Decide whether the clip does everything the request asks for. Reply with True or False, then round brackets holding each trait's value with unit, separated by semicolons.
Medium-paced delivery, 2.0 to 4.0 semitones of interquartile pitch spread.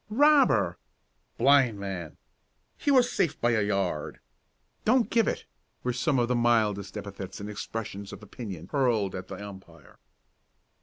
False (145 wpm; 4.4 semitones)